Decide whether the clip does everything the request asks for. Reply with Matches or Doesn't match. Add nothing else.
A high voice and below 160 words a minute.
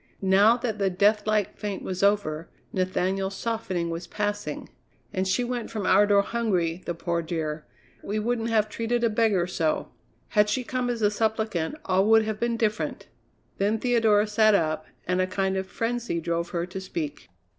Doesn't match